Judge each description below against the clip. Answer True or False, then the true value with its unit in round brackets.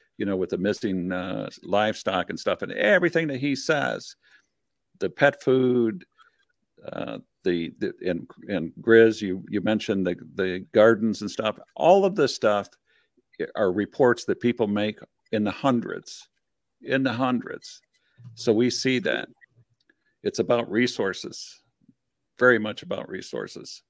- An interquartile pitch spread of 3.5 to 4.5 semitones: True (3.8 semitones)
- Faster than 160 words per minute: False (145 wpm)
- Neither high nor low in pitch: False (115 Hz)